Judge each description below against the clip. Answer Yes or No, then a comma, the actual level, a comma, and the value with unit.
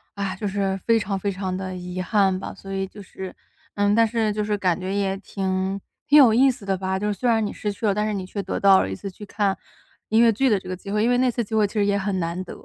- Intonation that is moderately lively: No, narrow, 2.1 semitones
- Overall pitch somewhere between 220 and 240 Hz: No, high, 200 Hz